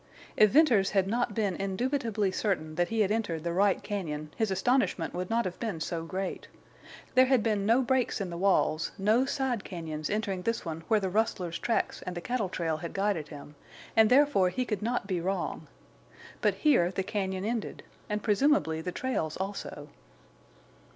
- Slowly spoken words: No, average, 185 wpm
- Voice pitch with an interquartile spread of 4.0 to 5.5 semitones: Yes, average, 4.4 semitones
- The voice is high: Yes, high, 195 Hz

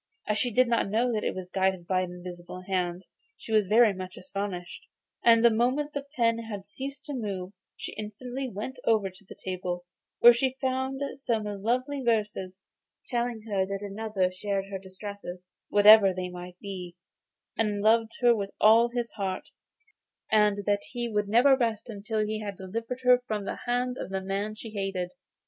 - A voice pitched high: Yes, high, 210 Hz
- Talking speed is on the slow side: No, average, 185 wpm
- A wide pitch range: No, average, 3.6 semitones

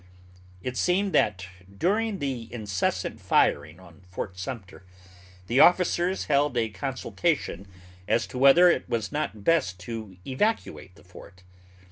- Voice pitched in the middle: No, low, 120 Hz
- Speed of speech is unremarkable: No, slow, 130 wpm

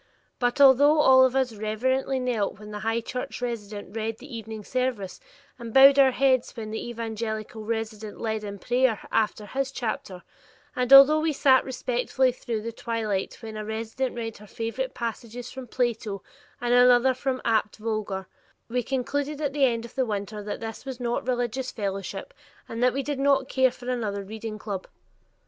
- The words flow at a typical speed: Yes, average, 180 wpm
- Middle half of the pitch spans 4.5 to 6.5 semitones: No, average, 3.2 semitones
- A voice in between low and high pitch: No, high, 235 Hz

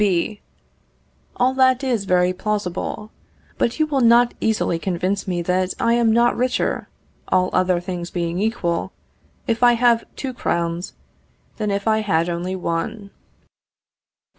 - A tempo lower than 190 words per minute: Yes, average, 140 wpm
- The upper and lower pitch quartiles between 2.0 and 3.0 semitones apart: No, average, 4.7 semitones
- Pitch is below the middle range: No, high, 200 Hz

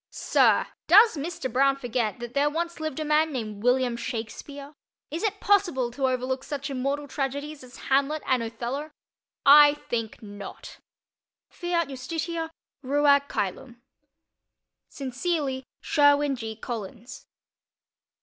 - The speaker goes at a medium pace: No, slow, 120 wpm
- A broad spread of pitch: No, average, 3.4 semitones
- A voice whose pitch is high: Yes, very high, 275 Hz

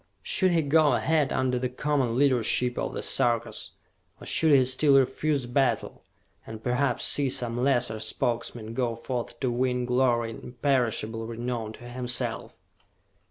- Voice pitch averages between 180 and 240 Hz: No, low, 125 Hz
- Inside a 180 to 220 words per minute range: No, average, 150 wpm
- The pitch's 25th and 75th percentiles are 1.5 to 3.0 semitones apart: Yes, narrow, 2.5 semitones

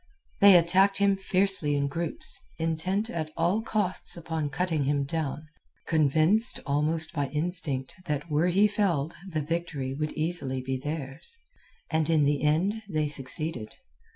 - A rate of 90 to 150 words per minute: Yes, average, 145 wpm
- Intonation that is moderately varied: Yes, average, 3.6 semitones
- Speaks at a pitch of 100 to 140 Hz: No, medium, 160 Hz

